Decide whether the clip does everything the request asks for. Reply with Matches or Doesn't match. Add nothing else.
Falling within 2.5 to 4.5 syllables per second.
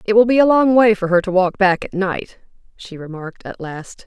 Doesn't match